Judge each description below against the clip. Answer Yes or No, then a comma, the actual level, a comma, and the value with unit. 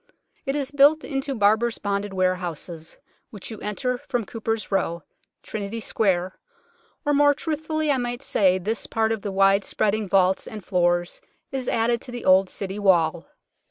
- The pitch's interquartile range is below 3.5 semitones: No, average, 4.6 semitones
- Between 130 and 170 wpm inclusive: Yes, average, 160 wpm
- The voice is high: Yes, high, 210 Hz